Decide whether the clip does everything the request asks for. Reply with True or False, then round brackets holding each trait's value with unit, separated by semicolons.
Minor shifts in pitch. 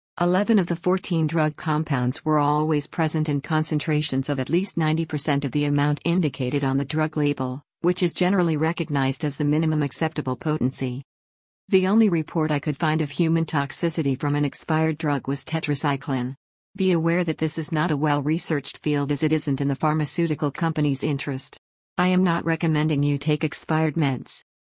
True (2.1 semitones)